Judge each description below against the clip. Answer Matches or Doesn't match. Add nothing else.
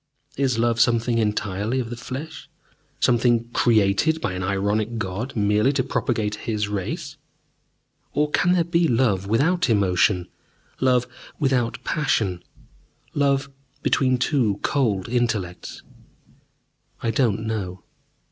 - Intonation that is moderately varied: Matches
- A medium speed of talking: Doesn't match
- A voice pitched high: Doesn't match